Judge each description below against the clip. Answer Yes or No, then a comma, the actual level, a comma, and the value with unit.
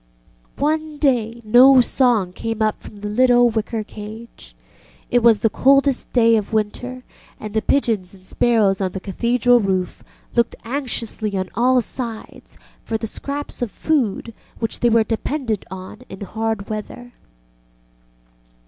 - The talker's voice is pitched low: No, high, 230 Hz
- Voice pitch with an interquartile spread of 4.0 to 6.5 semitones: No, average, 2.9 semitones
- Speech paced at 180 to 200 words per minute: No, average, 150 wpm